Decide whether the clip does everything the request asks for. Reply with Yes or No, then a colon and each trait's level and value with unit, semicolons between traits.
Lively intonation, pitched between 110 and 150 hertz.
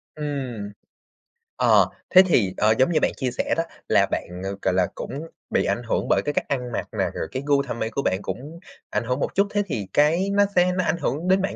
Yes: wide, 6.6 semitones; medium, 140 Hz